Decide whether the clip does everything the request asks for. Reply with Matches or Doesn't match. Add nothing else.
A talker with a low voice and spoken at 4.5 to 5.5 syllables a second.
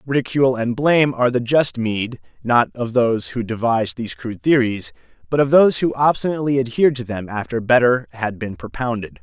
Doesn't match